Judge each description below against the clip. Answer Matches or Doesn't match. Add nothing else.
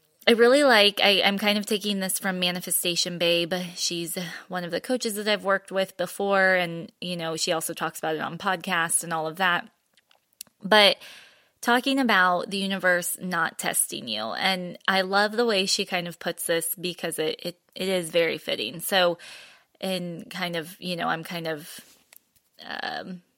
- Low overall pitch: Doesn't match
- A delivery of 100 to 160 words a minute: Doesn't match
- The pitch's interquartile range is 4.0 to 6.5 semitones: Doesn't match